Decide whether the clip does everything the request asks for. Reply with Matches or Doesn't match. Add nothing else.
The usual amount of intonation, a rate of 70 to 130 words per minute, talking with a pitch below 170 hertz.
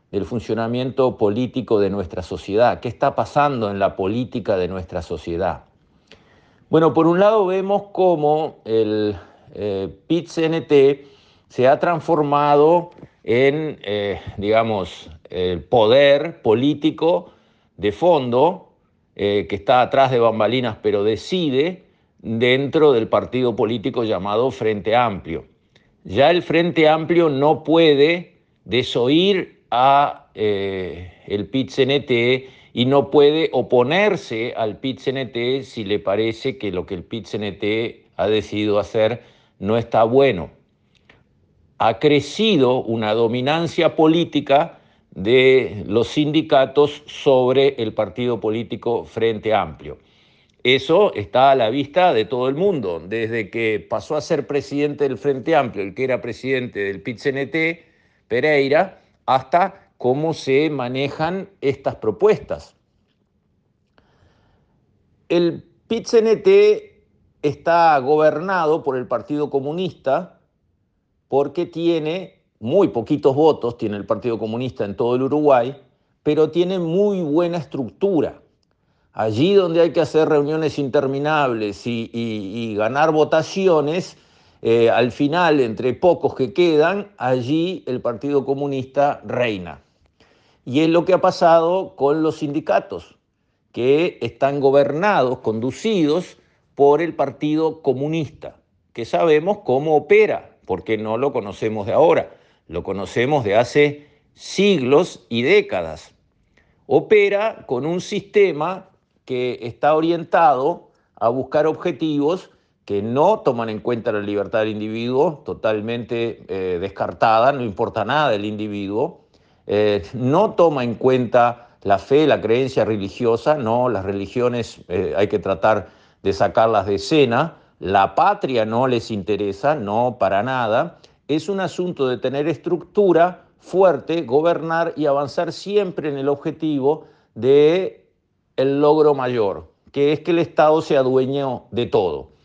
Doesn't match